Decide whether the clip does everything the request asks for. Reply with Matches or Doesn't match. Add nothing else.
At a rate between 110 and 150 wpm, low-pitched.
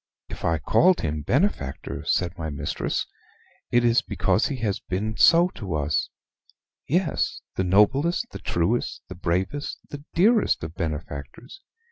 Matches